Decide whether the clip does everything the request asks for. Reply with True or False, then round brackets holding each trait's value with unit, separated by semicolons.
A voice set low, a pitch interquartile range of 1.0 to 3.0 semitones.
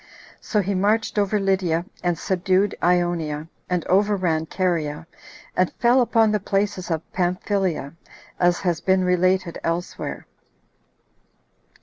False (185 Hz; 2.6 semitones)